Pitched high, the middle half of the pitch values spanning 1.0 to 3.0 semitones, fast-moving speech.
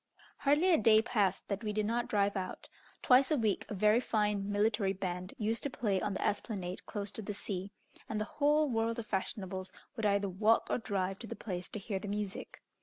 Yes: high, 210 Hz; narrow, 2.5 semitones; fast, 215 wpm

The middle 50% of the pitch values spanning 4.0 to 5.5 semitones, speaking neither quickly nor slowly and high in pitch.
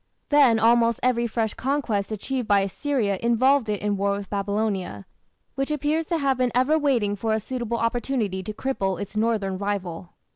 Yes: average, 4.4 semitones; average, 175 wpm; high, 225 Hz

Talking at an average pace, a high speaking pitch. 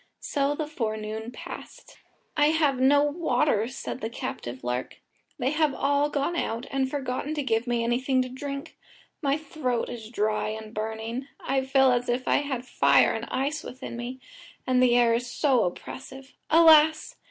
Yes: average, 170 wpm; very high, 260 Hz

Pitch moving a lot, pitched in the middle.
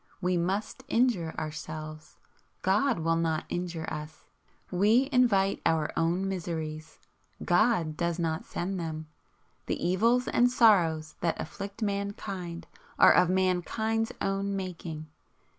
No: average, 3.7 semitones; medium, 180 Hz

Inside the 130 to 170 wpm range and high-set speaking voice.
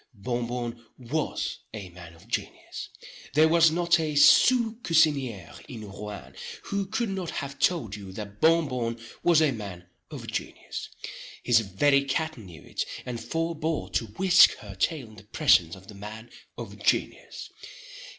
No: average, 160 wpm; low, 120 Hz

